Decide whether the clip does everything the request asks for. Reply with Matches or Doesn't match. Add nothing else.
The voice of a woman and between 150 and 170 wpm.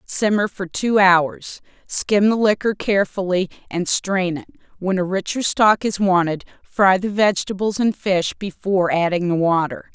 Matches